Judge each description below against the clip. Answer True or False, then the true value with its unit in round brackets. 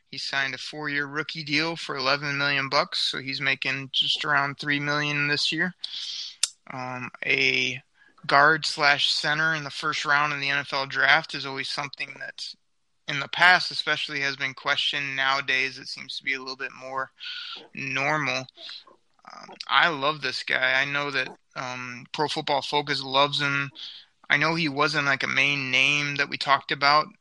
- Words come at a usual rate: True (175 wpm)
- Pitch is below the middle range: False (145 Hz)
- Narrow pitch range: True (2.0 semitones)